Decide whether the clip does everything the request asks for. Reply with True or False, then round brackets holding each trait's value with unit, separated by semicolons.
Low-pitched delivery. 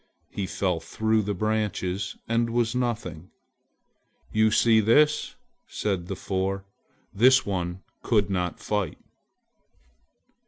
True (105 Hz)